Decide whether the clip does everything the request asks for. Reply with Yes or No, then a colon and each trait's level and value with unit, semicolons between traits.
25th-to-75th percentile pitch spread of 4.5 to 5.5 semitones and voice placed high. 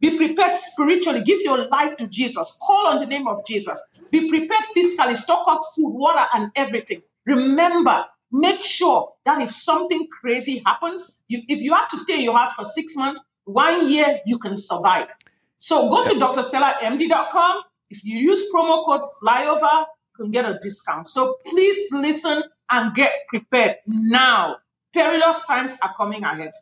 Yes: average, 5.2 semitones; very high, 295 Hz